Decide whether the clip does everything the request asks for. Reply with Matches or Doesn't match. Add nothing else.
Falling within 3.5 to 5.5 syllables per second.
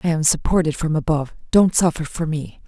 Doesn't match